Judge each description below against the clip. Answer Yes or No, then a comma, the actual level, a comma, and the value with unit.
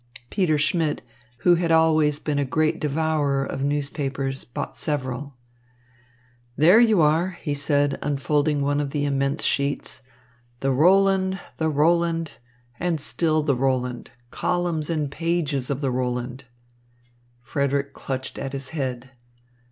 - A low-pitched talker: No, medium, 145 Hz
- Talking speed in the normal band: No, slow, 130 wpm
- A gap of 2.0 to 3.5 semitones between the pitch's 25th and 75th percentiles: Yes, average, 2.9 semitones